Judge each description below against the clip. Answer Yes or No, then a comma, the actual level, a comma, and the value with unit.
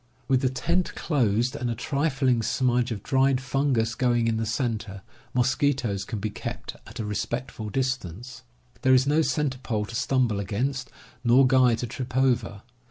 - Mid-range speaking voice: No, low, 125 Hz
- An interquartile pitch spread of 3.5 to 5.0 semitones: No, average, 2.9 semitones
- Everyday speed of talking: Yes, average, 165 wpm